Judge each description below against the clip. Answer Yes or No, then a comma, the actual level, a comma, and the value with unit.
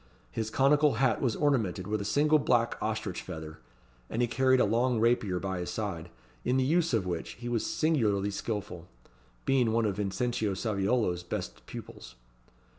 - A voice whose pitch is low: Yes, low, 115 Hz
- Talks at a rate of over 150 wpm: Yes, average, 170 wpm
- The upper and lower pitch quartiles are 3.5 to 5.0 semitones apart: Yes, average, 4.7 semitones